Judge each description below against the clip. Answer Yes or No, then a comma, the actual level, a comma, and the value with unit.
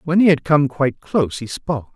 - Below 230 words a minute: No, fast, 245 wpm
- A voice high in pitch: No, medium, 145 Hz